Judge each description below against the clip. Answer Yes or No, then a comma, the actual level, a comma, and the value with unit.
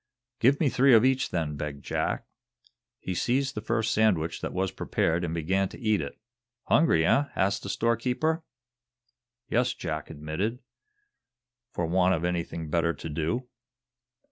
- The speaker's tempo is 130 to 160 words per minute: Yes, average, 150 wpm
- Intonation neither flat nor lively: No, wide, 6.7 semitones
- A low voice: Yes, very low, 95 Hz